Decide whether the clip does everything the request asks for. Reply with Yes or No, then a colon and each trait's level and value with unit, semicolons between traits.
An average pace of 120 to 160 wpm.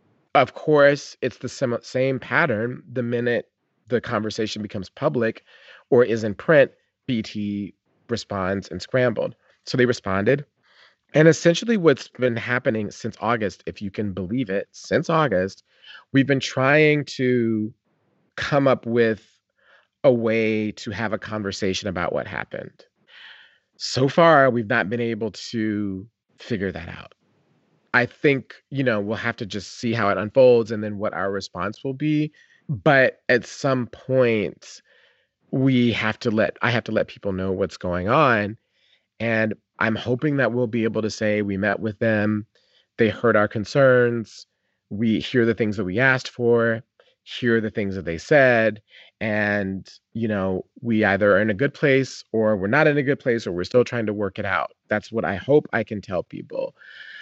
No: average, 170 wpm